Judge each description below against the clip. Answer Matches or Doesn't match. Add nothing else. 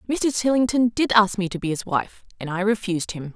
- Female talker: Matches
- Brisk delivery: Matches